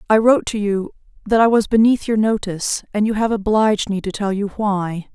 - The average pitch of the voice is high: Yes, high, 210 Hz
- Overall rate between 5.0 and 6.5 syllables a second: Yes, 5.5 syllables/s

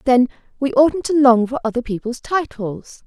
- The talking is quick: No, average, 175 wpm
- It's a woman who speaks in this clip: Yes, female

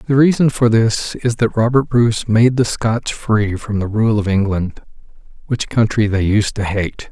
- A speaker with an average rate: Yes, average, 195 wpm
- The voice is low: Yes, low, 110 Hz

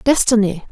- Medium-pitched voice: No, high, 215 Hz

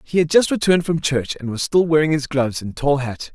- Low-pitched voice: No, medium, 150 Hz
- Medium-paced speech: No, fast, 270 wpm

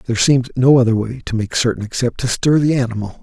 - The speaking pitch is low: Yes, low, 120 Hz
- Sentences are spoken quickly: Yes, fast, 240 wpm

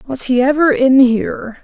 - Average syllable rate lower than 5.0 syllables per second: Yes, 4.7 syllables/s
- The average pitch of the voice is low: No, very high, 260 Hz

